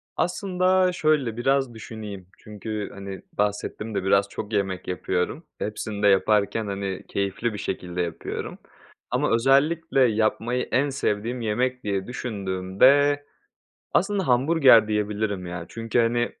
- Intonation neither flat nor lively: Yes, average, 4.5 semitones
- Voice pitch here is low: Yes, low, 110 Hz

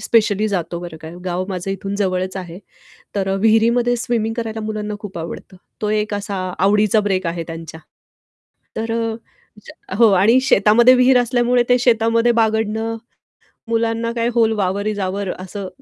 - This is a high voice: Yes, high, 215 Hz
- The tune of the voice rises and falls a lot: No, average, 3.2 semitones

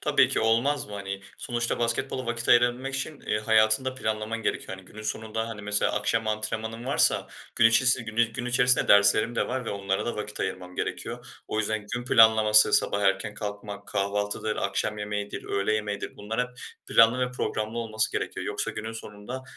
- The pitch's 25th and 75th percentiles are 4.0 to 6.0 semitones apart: No, narrow, 2.4 semitones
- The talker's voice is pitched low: Yes, low, 110 Hz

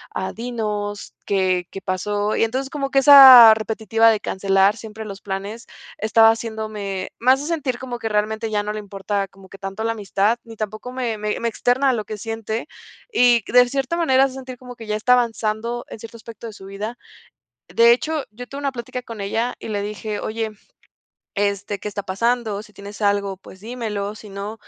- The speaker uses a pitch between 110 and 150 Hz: No, high, 220 Hz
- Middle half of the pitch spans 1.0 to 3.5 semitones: Yes, average, 2.9 semitones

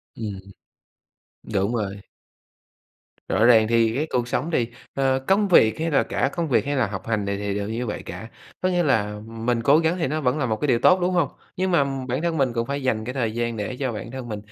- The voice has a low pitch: Yes, low, 125 Hz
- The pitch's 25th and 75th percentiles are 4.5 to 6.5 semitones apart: Yes, average, 5.1 semitones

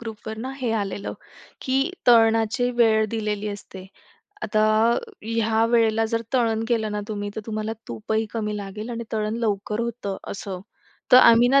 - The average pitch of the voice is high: Yes, high, 220 Hz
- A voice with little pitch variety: Yes, narrow, 1.6 semitones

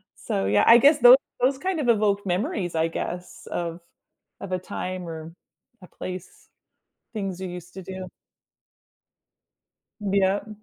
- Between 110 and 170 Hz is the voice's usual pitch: No, medium, 185 Hz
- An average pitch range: Yes, average, 3.5 semitones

